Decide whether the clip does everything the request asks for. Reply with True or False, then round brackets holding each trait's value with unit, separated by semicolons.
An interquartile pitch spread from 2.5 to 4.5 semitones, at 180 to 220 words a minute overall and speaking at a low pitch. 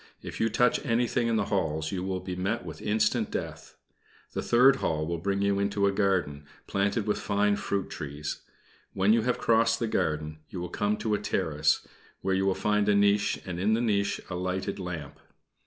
True (3.0 semitones; 200 wpm; 100 Hz)